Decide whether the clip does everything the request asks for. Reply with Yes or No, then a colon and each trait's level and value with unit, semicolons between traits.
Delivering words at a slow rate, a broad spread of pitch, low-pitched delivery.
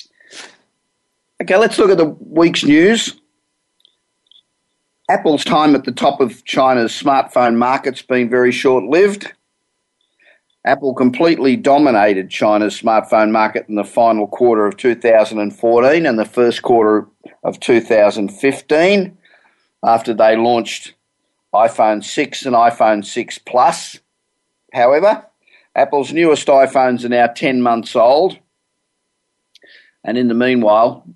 No: slow, 115 wpm; average, 4.0 semitones; low, 120 Hz